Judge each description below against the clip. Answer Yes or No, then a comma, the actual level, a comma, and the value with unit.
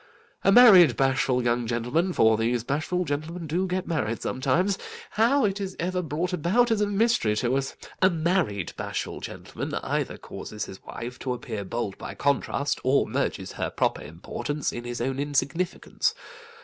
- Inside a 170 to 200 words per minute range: No, average, 155 wpm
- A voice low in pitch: No, medium, 145 Hz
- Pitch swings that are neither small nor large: No, wide, 7.2 semitones